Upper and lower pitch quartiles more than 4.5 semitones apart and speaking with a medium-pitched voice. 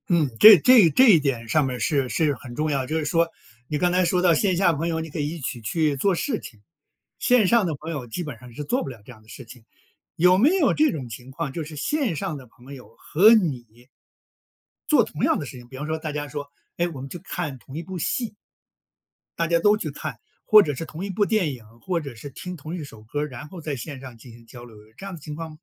Yes: average, 5.2 semitones; medium, 155 Hz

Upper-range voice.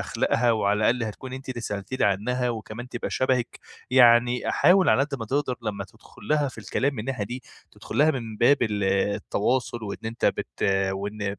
No: low, 120 Hz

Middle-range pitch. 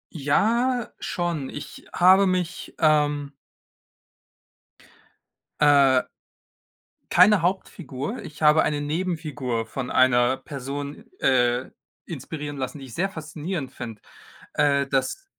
Yes: medium, 145 Hz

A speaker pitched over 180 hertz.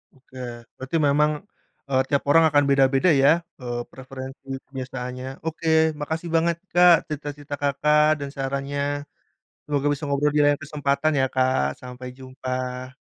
No: medium, 140 Hz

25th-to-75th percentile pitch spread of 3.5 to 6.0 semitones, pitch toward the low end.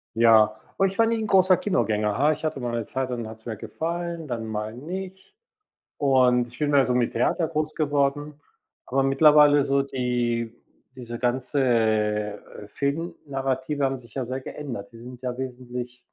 Yes: average, 3.8 semitones; low, 130 Hz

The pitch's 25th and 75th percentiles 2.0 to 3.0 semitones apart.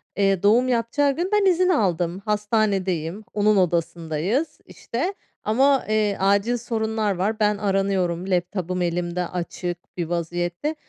No: average, 4.4 semitones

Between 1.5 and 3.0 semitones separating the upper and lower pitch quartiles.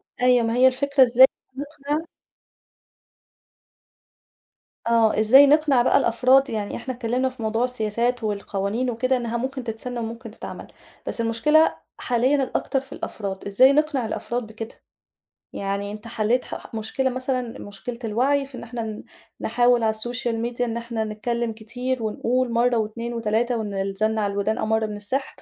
Yes: average, 2.7 semitones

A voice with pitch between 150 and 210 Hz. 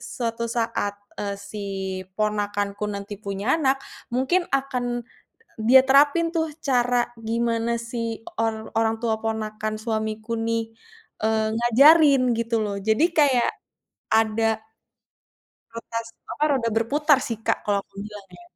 No: high, 230 Hz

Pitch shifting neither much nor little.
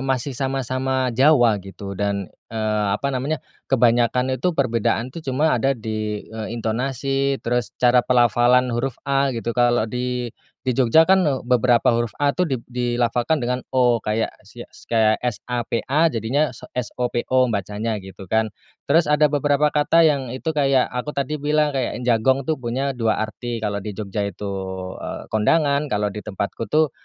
Yes: average, 3.5 semitones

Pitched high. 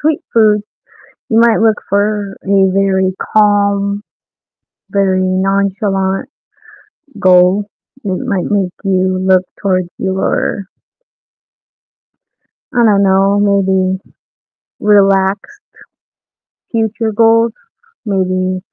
Yes: high, 195 Hz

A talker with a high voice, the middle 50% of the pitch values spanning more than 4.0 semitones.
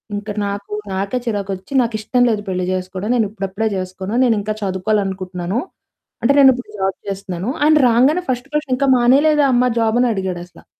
Yes: high, 210 Hz; average, 4.4 semitones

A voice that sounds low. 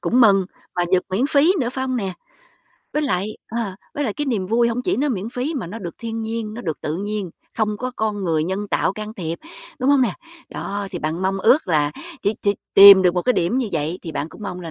No: high, 205 Hz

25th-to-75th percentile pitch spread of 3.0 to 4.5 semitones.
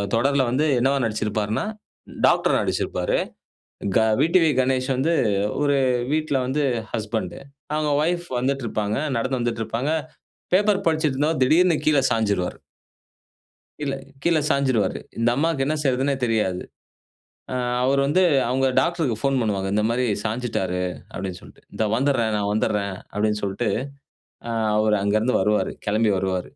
No: average, 5.2 semitones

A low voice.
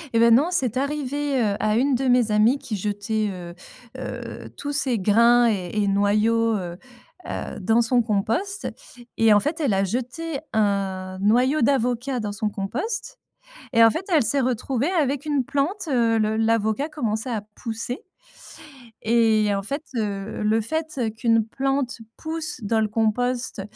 No: high, 230 Hz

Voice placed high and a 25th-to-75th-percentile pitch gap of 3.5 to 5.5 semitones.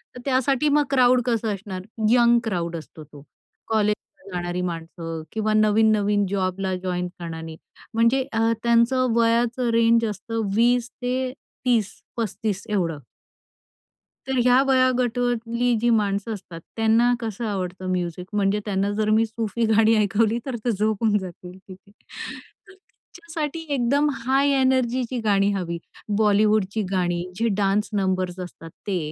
Yes: high, 220 Hz; average, 4.1 semitones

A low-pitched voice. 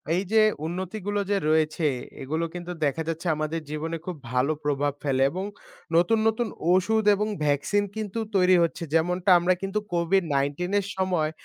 No: medium, 175 Hz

